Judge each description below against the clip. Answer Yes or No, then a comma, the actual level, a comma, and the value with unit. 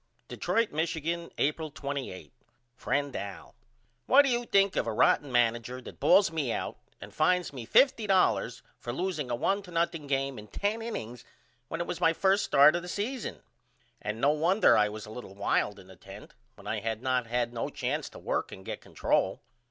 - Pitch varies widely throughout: Yes, wide, 7.4 semitones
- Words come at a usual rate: Yes, average, 190 wpm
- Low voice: No, medium, 145 Hz